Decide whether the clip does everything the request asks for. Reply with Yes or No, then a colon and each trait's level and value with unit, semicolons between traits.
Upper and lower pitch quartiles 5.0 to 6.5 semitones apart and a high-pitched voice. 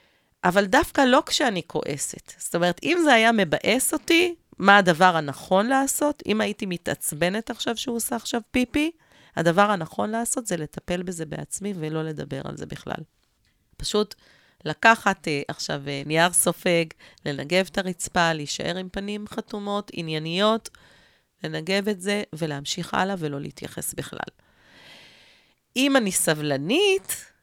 Yes: wide, 5.5 semitones; high, 200 Hz